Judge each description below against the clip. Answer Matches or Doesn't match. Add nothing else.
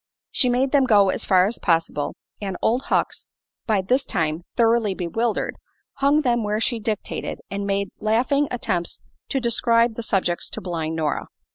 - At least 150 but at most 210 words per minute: Matches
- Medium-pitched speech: Doesn't match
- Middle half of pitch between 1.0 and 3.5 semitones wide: Doesn't match